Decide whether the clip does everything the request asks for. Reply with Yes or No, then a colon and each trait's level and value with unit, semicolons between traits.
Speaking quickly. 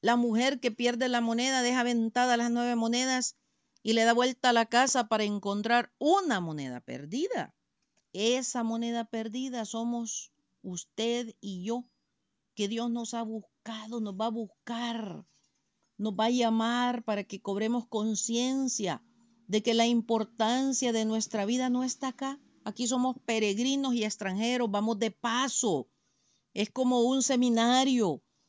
No: average, 145 wpm